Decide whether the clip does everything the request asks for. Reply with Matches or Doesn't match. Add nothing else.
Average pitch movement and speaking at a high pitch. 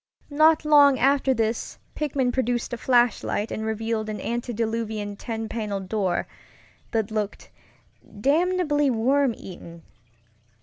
Matches